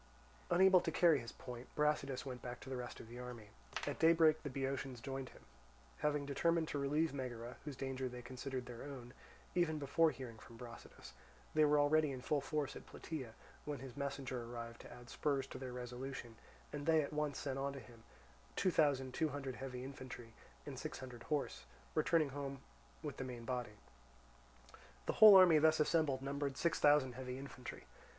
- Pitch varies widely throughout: No, average, 3.1 semitones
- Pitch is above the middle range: No, low, 135 Hz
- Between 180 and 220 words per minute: Yes, average, 185 wpm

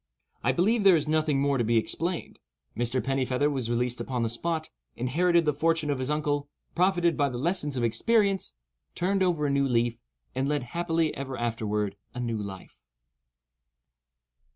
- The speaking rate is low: No, average, 170 wpm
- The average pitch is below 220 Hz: Yes, medium, 140 Hz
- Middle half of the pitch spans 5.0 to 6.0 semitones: Yes, wide, 5.4 semitones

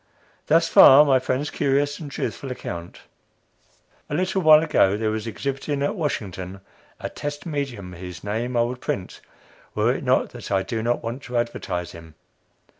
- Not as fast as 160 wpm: No, average, 170 wpm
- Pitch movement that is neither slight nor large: No, wide, 6.4 semitones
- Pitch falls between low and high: No, low, 120 Hz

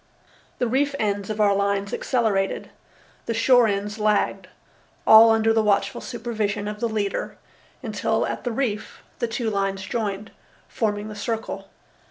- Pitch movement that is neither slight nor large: No, narrow, 2.1 semitones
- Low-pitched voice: No, high, 215 Hz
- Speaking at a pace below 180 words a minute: Yes, average, 150 wpm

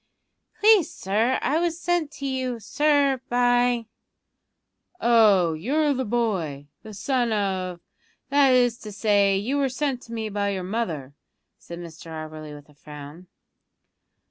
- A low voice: No, high, 225 Hz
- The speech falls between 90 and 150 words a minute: Yes, average, 145 wpm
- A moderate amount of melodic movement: No, wide, 6.5 semitones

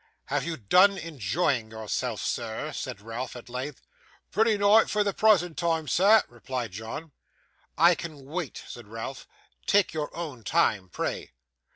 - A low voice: No, medium, 150 Hz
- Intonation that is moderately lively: No, wide, 7.0 semitones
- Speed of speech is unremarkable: Yes, average, 150 wpm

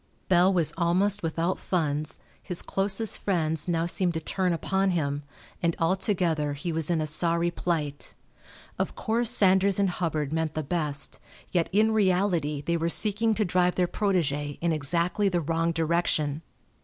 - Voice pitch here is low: No, medium, 170 Hz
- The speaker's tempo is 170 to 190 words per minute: No, average, 160 wpm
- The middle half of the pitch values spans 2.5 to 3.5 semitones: Yes, average, 3.1 semitones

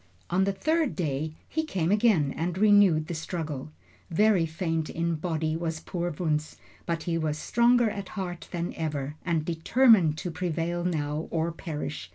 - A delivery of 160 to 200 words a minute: Yes, average, 165 wpm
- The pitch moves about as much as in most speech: Yes, average, 3.3 semitones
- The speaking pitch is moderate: Yes, medium, 170 Hz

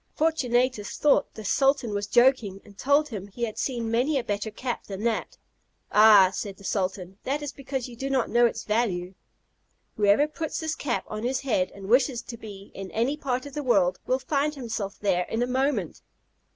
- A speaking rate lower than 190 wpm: No, average, 200 wpm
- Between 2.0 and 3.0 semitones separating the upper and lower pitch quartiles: No, average, 4.8 semitones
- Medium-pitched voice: No, high, 235 Hz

